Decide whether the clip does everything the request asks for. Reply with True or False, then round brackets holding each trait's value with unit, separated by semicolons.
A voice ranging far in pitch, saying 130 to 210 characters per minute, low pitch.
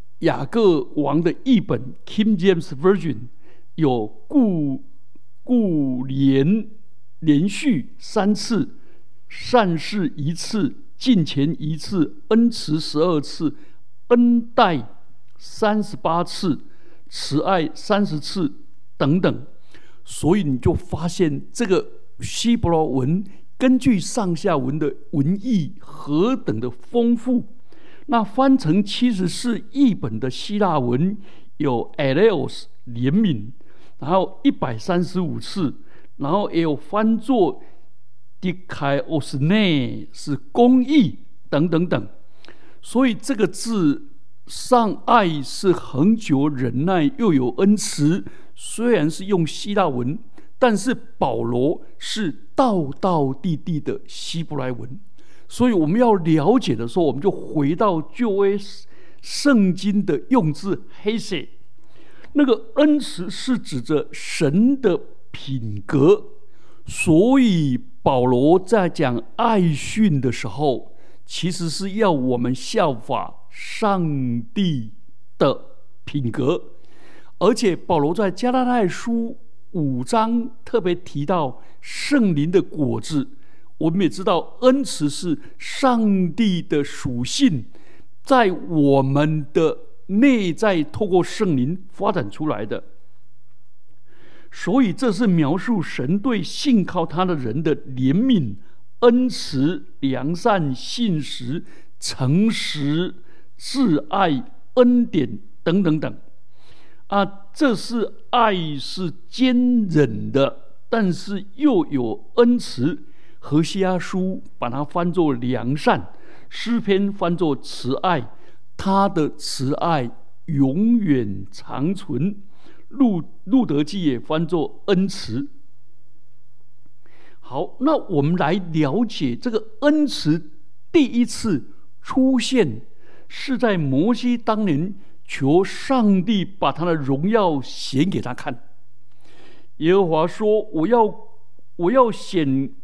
False (8.0 semitones; 165 characters per minute; 175 Hz)